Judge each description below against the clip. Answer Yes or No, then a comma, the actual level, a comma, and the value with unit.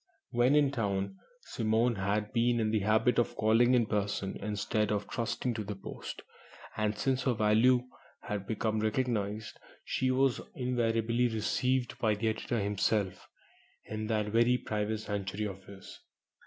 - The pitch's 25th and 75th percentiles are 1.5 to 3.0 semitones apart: Yes, narrow, 2.6 semitones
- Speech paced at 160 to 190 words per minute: No, average, 150 wpm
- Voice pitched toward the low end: Yes, low, 110 Hz